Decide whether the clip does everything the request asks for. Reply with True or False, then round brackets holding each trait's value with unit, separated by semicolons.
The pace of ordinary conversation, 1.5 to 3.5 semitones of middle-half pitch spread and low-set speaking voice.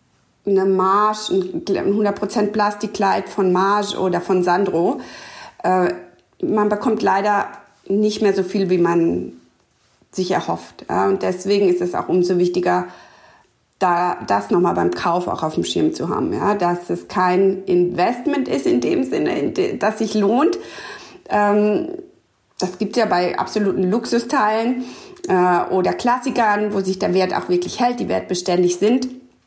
False (155 wpm; 2.9 semitones; 195 Hz)